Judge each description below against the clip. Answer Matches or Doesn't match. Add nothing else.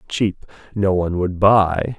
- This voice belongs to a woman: Doesn't match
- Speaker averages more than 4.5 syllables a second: Doesn't match